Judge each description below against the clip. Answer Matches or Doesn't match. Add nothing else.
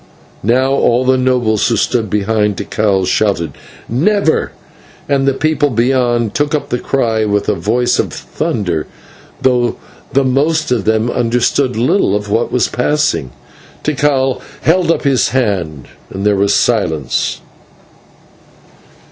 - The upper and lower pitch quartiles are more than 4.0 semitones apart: Matches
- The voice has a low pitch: Matches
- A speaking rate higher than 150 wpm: Doesn't match